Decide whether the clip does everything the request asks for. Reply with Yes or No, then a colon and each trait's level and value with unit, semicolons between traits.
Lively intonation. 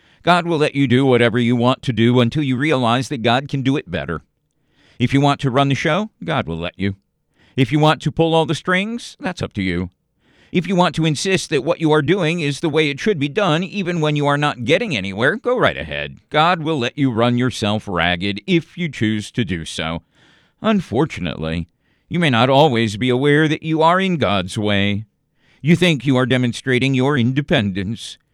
Yes: wide, 5.8 semitones